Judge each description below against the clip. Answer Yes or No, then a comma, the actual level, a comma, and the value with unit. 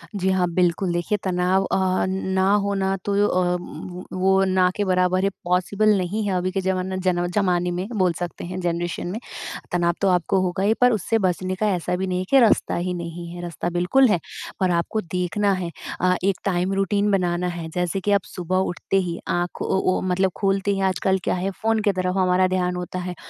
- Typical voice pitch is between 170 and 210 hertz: Yes, medium, 185 Hz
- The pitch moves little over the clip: Yes, narrow, 1.5 semitones